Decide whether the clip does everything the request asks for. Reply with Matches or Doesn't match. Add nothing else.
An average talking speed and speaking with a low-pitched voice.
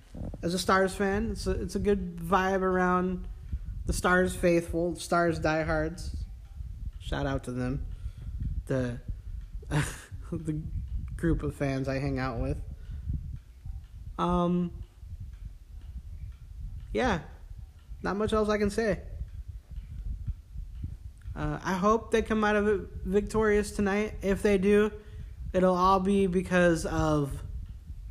Doesn't match